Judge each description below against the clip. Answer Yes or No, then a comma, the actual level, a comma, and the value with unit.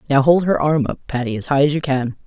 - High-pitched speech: No, medium, 140 Hz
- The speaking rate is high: Yes, fast, 290 wpm